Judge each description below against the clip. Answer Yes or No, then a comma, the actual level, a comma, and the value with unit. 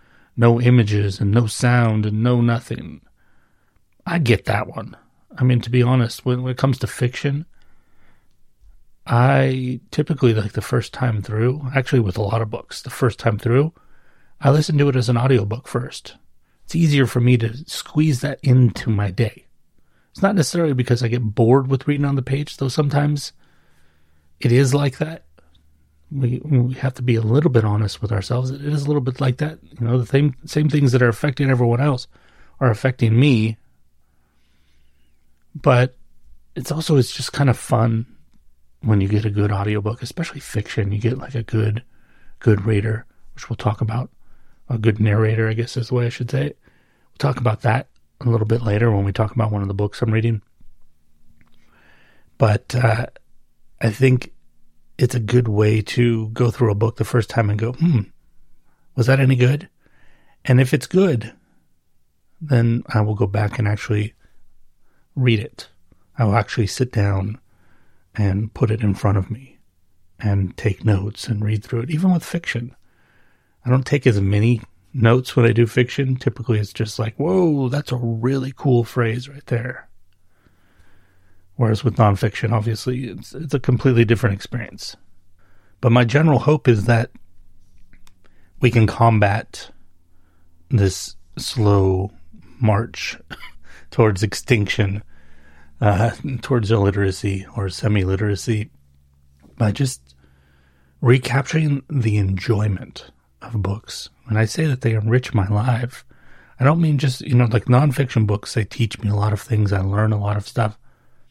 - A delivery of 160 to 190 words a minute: Yes, average, 170 wpm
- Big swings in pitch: No, average, 4.1 semitones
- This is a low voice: Yes, low, 115 Hz